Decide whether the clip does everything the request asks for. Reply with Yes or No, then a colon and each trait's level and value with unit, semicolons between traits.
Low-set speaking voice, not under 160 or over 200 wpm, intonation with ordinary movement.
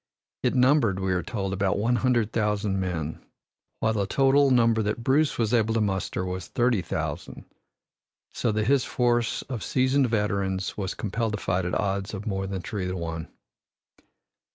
Yes: low, 105 Hz; average, 175 wpm; average, 3.8 semitones